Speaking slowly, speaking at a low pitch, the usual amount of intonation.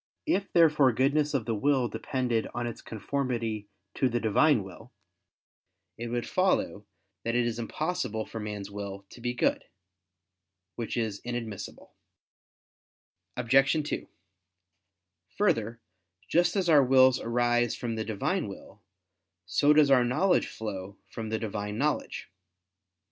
Yes: slow, 130 wpm; low, 120 Hz; average, 4.0 semitones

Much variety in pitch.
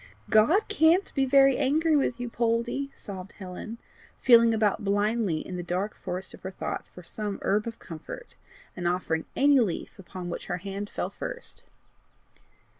Yes: wide, 6.2 semitones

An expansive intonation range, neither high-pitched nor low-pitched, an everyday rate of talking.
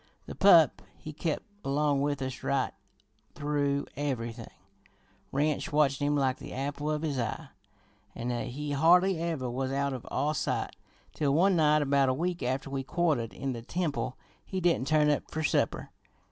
No: narrow, 2.4 semitones; medium, 145 Hz; average, 170 wpm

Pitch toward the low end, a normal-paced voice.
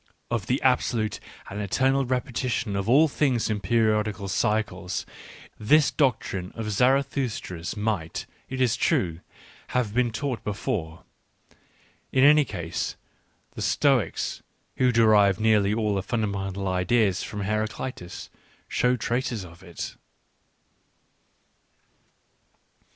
No: low, 110 Hz; slow, 120 wpm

